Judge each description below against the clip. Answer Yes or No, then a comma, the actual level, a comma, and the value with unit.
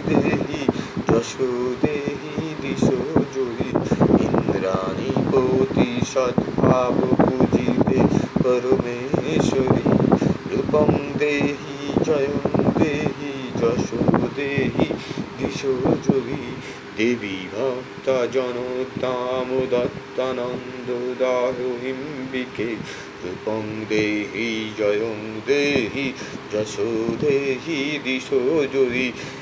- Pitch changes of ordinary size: No, narrow, 2.1 semitones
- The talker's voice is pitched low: Yes, low, 130 Hz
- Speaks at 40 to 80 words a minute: Yes, average, 45 wpm